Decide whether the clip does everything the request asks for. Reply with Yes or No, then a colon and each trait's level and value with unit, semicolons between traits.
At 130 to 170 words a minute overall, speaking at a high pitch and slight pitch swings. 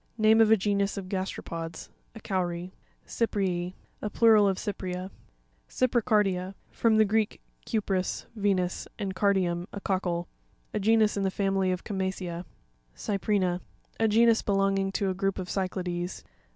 Yes: average, 145 wpm; high, 195 Hz; narrow, 2.3 semitones